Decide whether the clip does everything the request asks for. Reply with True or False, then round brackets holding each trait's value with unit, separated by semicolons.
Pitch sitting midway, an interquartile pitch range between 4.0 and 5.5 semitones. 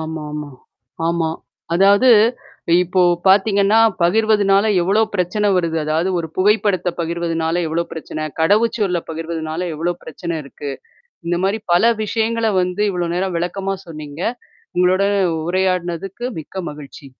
False (180 Hz; 3.3 semitones)